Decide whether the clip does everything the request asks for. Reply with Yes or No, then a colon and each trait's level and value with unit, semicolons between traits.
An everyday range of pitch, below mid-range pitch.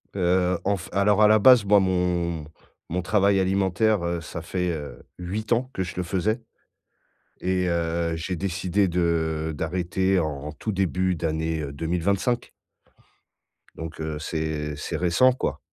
Yes: average, 3.0 semitones; very low, 90 Hz